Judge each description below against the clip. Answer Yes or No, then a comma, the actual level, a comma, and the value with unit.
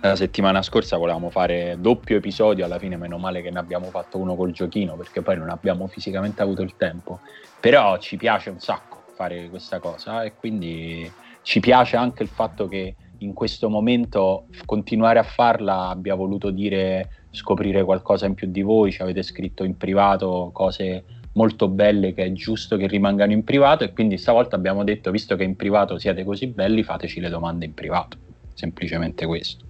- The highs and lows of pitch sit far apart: No, narrow, 2.4 semitones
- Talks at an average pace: No, fast, 185 wpm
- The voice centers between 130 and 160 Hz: No, very low, 95 Hz